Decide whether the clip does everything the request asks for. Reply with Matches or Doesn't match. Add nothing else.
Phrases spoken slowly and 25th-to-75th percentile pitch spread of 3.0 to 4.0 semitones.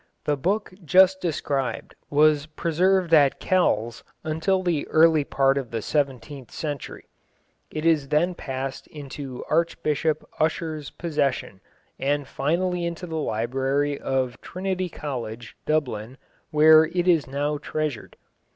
Matches